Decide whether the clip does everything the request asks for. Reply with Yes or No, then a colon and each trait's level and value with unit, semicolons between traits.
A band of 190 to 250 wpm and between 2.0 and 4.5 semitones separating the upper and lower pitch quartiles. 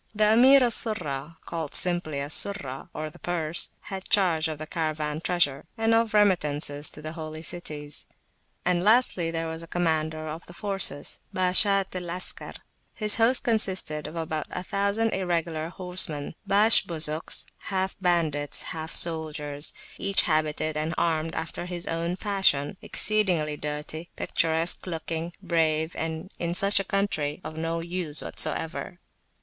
No: average, 145 wpm; average, 3.3 semitones